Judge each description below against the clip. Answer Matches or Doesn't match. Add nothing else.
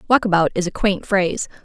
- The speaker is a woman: Matches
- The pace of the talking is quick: Matches